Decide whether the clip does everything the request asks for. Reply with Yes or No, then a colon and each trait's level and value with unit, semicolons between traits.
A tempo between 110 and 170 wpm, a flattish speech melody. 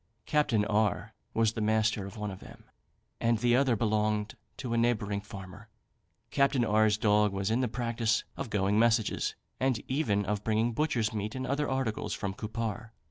No: average, 180 wpm; narrow, 2.1 semitones